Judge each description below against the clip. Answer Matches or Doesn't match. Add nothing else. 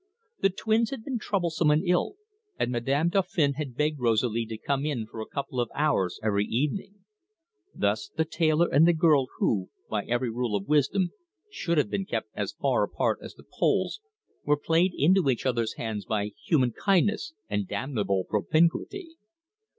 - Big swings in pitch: Matches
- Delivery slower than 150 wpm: Doesn't match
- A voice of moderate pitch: Matches